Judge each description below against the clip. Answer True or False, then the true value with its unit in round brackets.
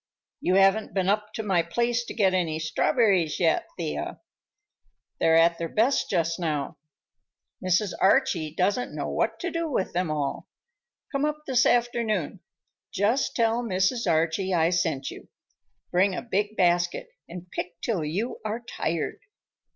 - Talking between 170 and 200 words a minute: False (150 wpm)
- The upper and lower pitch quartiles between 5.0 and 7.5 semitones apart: True (5.3 semitones)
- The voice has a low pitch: False (190 Hz)